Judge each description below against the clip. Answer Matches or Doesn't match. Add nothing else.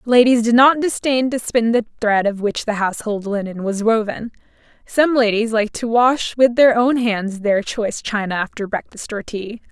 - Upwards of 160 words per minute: Matches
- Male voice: Doesn't match